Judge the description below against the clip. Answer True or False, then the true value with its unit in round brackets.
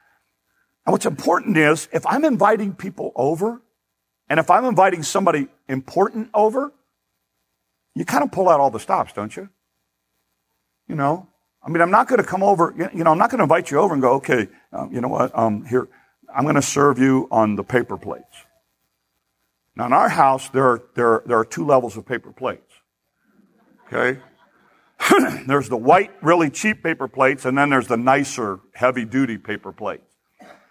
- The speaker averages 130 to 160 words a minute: False (185 wpm)